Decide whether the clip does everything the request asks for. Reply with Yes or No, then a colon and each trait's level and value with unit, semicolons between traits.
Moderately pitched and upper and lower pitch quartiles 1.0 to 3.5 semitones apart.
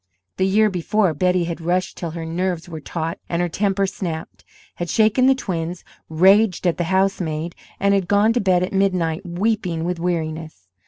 Yes: medium, 180 Hz; average, 2.9 semitones